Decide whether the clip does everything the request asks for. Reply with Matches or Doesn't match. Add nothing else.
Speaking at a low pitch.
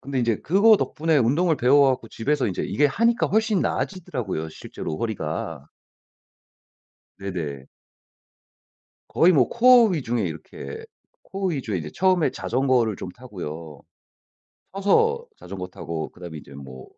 Matches